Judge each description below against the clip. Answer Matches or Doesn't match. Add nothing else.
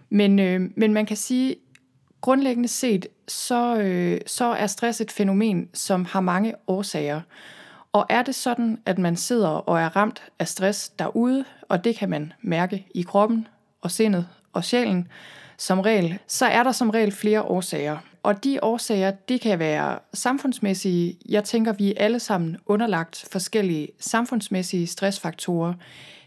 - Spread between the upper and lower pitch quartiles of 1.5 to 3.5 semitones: Doesn't match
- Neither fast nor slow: Matches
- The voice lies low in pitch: Doesn't match